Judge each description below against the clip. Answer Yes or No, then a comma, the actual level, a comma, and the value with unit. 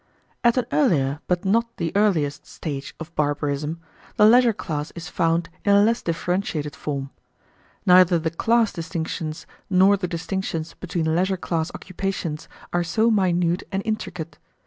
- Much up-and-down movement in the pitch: No, average, 3.8 semitones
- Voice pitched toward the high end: No, medium, 175 Hz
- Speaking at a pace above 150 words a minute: No, average, 145 wpm